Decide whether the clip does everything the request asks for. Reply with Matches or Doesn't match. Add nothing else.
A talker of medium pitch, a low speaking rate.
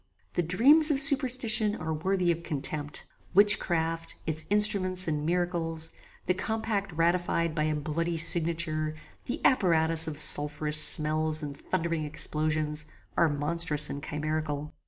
Matches